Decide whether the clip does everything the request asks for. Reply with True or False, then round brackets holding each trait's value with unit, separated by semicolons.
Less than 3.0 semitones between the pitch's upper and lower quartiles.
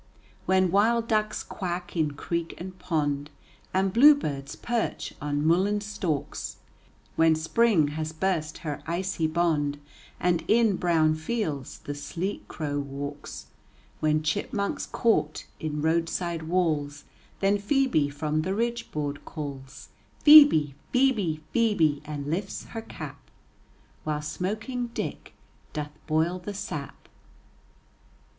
False (5.0 semitones)